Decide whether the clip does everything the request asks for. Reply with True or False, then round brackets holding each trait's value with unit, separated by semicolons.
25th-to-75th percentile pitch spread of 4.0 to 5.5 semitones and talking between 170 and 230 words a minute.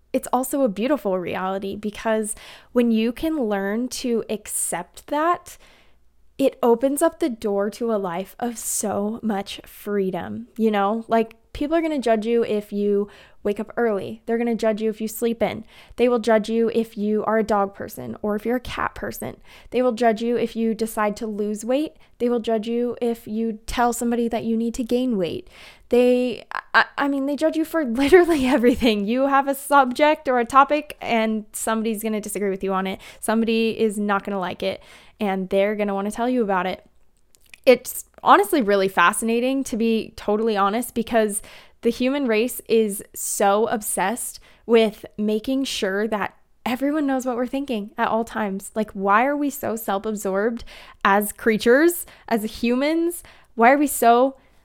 False (3.0 semitones; 185 wpm)